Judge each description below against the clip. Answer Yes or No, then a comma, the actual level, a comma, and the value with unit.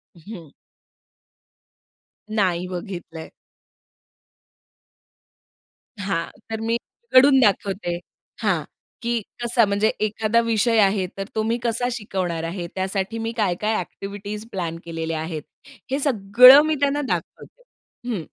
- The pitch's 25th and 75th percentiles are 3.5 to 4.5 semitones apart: Yes, average, 4.2 semitones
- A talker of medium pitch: No, high, 205 Hz